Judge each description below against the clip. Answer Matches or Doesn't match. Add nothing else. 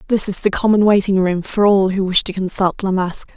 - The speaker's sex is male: Doesn't match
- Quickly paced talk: Matches